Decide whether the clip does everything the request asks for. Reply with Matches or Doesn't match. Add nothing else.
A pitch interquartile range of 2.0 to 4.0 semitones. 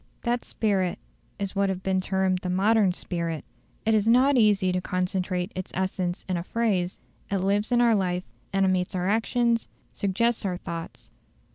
Matches